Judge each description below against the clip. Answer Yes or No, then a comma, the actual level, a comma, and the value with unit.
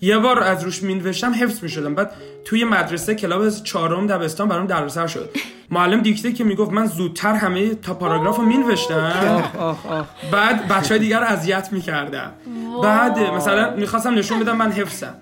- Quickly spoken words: Yes, fast, 165 wpm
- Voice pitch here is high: Yes, high, 200 Hz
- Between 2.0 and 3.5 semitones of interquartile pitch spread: No, average, 4.0 semitones